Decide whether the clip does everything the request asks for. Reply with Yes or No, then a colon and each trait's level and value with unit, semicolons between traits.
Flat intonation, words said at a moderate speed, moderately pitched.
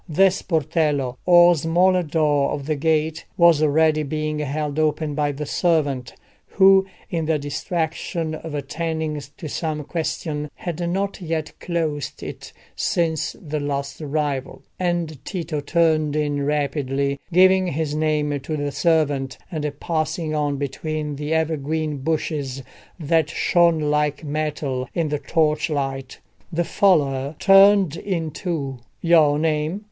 No: narrow, 2.2 semitones; slow, 130 wpm; medium, 155 Hz